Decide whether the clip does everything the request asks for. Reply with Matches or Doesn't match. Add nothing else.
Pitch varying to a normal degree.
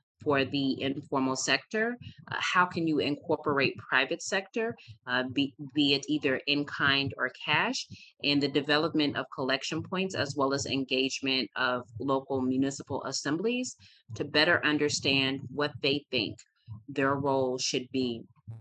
Doesn't match